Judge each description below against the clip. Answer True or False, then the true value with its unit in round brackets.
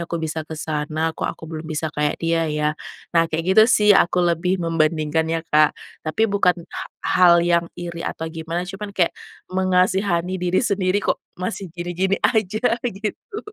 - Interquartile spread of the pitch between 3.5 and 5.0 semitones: False (2.7 semitones)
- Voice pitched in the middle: True (170 Hz)